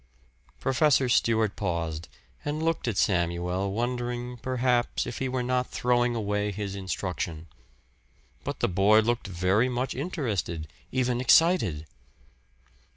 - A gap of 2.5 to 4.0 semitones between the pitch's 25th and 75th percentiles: No, average, 4.9 semitones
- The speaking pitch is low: Yes, low, 115 Hz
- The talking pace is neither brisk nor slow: No, slow, 120 wpm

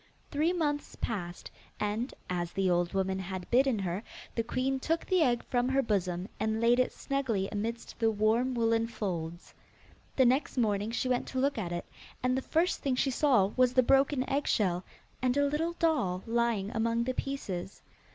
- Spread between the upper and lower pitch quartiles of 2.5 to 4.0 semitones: No, average, 5.3 semitones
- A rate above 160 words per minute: Yes, average, 180 wpm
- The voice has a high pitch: Yes, high, 235 Hz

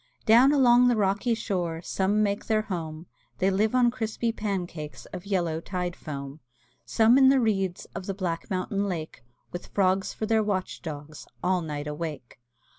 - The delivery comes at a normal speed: Yes, average, 170 wpm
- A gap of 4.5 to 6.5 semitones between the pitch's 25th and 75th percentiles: Yes, average, 4.8 semitones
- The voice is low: No, high, 190 Hz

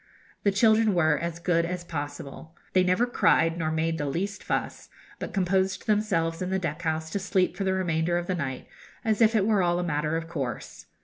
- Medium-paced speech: No, fast, 210 wpm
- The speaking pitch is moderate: Yes, medium, 175 Hz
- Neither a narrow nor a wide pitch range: Yes, average, 3.0 semitones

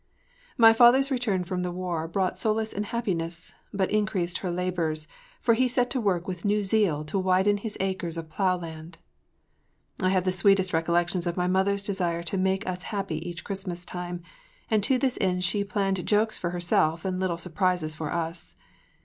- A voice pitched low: No, medium, 185 Hz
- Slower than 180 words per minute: No, average, 185 wpm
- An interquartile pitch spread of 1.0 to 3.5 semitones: Yes, average, 2.8 semitones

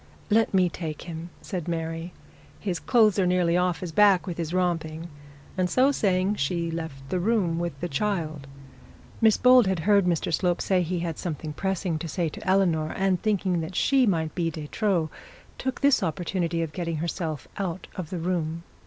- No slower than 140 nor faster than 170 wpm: No, average, 190 wpm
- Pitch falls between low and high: Yes, medium, 175 Hz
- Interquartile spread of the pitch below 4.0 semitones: Yes, average, 2.7 semitones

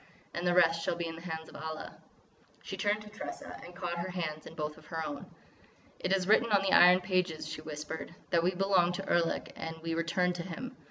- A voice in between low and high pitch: Yes, medium, 175 Hz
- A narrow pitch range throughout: Yes, narrow, 2.3 semitones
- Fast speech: Yes, fast, 230 wpm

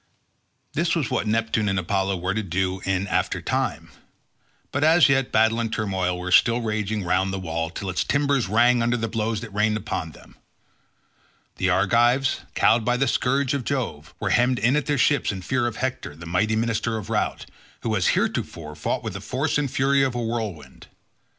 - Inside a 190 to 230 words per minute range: Yes, average, 195 wpm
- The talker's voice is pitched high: No, low, 110 Hz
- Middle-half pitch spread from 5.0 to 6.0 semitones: No, average, 4.6 semitones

